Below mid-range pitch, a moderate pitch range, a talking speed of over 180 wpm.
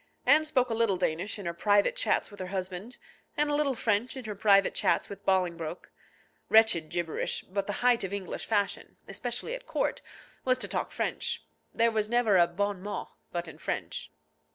No: high, 205 Hz; average, 4.2 semitones; average, 190 wpm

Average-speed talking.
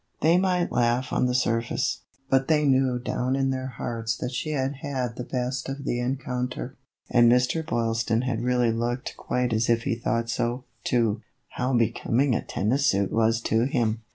Yes: average, 185 wpm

